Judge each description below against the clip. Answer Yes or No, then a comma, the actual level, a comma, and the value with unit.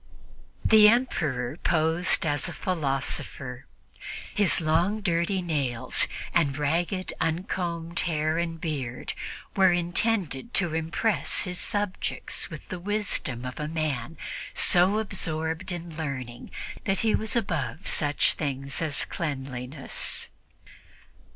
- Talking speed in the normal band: No, slow, 110 wpm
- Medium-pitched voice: Yes, medium, 165 Hz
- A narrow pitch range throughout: No, average, 4.3 semitones